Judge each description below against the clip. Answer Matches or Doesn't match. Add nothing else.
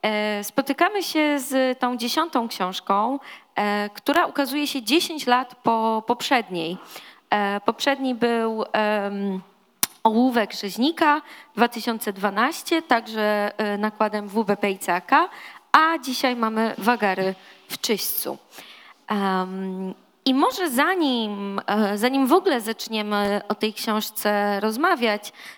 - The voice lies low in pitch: Doesn't match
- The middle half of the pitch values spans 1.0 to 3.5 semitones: Doesn't match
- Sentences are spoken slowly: Matches